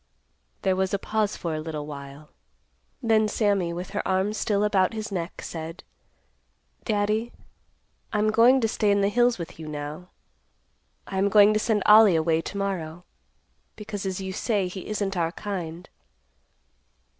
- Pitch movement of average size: Yes, average, 3.9 semitones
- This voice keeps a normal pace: Yes, average, 160 wpm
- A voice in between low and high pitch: No, high, 195 Hz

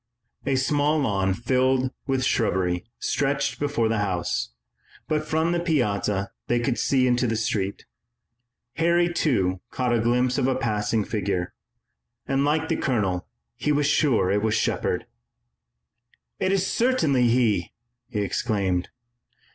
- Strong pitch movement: Yes, wide, 5.7 semitones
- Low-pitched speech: Yes, low, 125 Hz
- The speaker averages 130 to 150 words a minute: Yes, average, 140 wpm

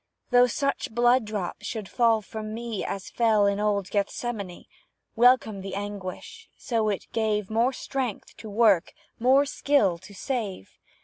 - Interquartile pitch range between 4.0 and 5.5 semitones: No, average, 3.2 semitones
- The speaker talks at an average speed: Yes, average, 145 wpm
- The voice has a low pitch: No, high, 220 Hz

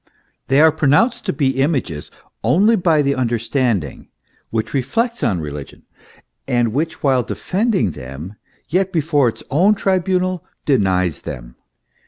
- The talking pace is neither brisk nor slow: No, slow, 130 wpm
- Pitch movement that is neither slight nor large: No, wide, 8.6 semitones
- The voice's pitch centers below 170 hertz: Yes, medium, 140 Hz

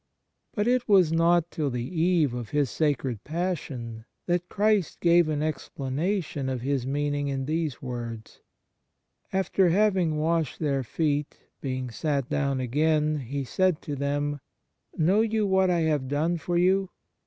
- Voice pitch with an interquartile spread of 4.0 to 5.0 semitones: Yes, average, 4.3 semitones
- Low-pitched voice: No, medium, 150 Hz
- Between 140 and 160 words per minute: Yes, average, 155 wpm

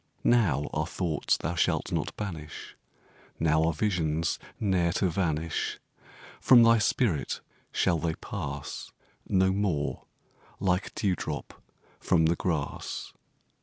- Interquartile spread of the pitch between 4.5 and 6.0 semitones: No, average, 3.5 semitones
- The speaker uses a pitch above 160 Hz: No, very low, 85 Hz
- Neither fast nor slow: No, slow, 120 wpm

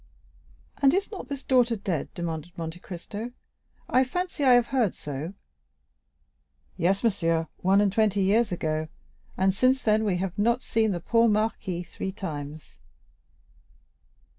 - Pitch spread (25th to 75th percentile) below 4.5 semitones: No, wide, 5.4 semitones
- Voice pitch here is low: No, high, 200 Hz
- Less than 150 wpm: Yes, average, 140 wpm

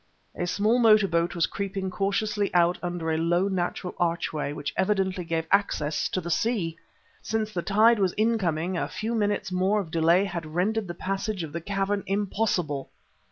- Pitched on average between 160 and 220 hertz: Yes, medium, 185 Hz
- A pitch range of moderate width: Yes, average, 3.3 semitones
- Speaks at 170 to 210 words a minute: Yes, average, 175 wpm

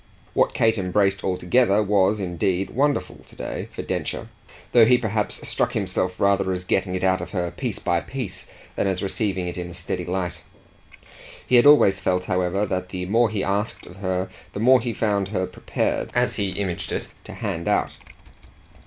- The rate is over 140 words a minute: Yes, average, 190 wpm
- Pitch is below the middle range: Yes, very low, 95 Hz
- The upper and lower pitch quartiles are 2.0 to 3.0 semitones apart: Yes, narrow, 2.6 semitones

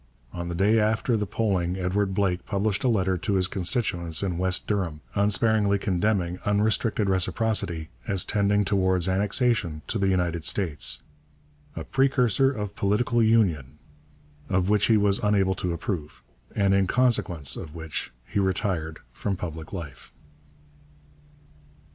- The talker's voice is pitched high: No, very low, 95 Hz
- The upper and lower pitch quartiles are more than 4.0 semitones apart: No, average, 3.1 semitones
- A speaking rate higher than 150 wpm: No, average, 140 wpm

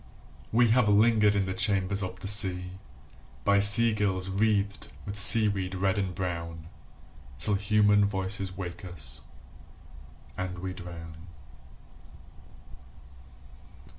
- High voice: No, very low, 95 Hz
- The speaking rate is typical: No, slow, 110 wpm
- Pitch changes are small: Yes, narrow, 2.1 semitones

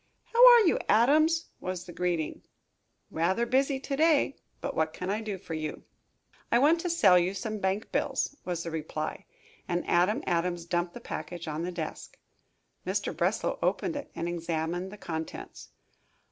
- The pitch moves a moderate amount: No, wide, 6.1 semitones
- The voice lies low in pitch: No, medium, 180 Hz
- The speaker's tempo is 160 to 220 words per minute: Yes, average, 170 wpm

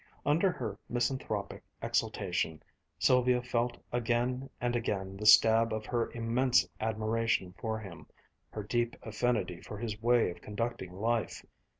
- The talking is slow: Yes, slow, 130 wpm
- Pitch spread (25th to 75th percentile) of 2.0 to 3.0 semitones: Yes, narrow, 2.4 semitones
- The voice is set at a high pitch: No, low, 115 Hz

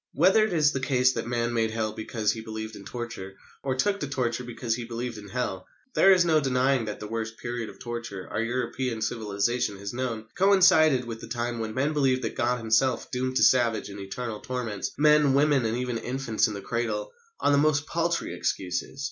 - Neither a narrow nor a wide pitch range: Yes, average, 3.1 semitones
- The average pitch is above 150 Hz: No, low, 120 Hz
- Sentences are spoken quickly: Yes, fast, 210 wpm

